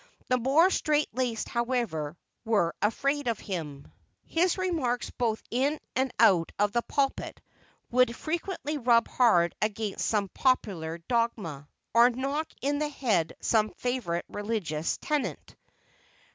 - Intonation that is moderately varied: Yes, average, 5.0 semitones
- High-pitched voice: Yes, high, 235 Hz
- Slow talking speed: Yes, slow, 130 wpm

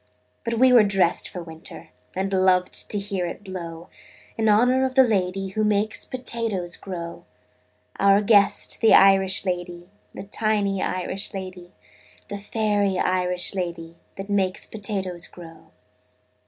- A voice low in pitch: No, high, 195 Hz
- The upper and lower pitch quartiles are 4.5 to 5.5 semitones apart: No, narrow, 2.5 semitones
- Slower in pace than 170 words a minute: Yes, average, 140 wpm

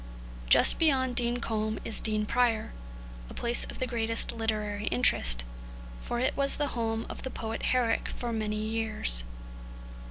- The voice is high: Yes, high, 225 Hz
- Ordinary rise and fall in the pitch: No, narrow, 2.2 semitones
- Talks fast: No, average, 155 wpm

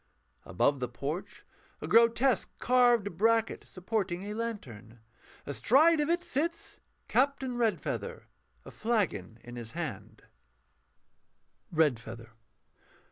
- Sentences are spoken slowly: Yes, slow, 105 wpm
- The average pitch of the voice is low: No, high, 205 Hz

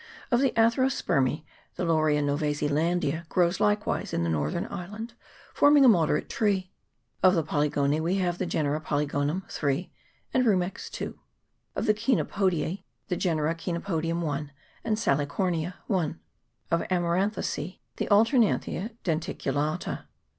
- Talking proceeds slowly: Yes, slow, 130 wpm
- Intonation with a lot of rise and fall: No, average, 4.7 semitones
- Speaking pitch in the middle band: Yes, medium, 170 Hz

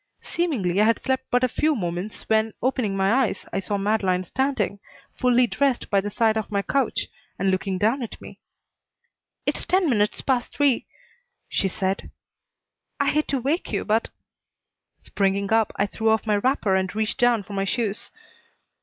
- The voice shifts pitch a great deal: No, average, 4.3 semitones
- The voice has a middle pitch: No, high, 220 Hz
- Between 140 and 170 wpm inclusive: No, average, 180 wpm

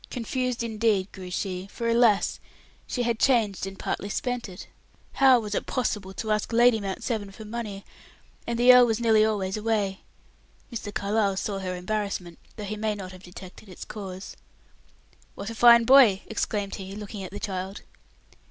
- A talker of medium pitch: No, high, 210 Hz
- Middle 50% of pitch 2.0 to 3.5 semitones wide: Yes, average, 3.1 semitones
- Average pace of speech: Yes, average, 175 wpm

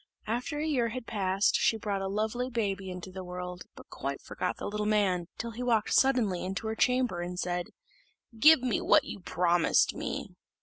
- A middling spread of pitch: Yes, average, 4.6 semitones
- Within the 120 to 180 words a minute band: No, average, 190 wpm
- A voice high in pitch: Yes, high, 210 Hz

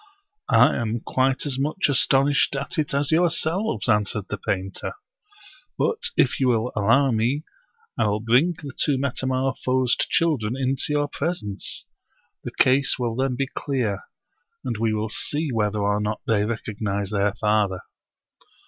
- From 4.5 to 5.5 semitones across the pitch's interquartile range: Yes, average, 4.8 semitones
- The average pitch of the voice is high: No, low, 130 Hz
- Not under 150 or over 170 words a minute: Yes, average, 155 wpm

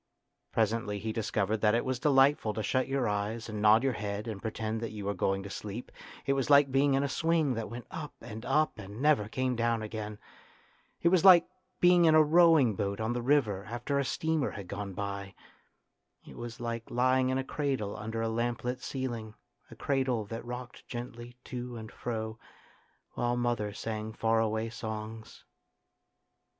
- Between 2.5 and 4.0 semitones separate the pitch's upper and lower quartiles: Yes, average, 3.4 semitones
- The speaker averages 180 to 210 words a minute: Yes, average, 185 wpm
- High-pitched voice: No, low, 115 Hz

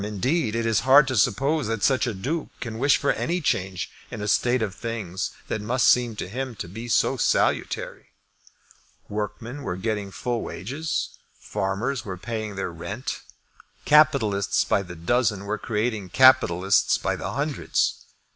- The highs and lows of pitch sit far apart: No, average, 4.7 semitones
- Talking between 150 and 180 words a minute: Yes, average, 160 wpm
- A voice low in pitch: Yes, low, 115 Hz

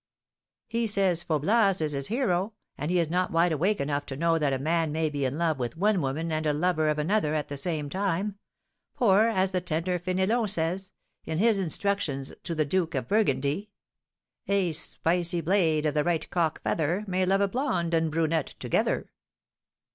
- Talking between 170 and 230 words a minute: Yes, average, 190 wpm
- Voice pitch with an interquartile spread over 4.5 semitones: No, average, 4.0 semitones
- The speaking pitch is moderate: Yes, medium, 170 Hz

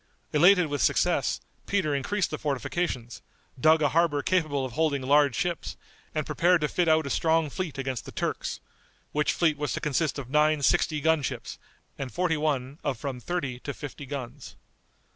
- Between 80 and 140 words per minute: No, average, 180 wpm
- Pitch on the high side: No, medium, 150 Hz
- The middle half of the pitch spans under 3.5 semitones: Yes, average, 2.8 semitones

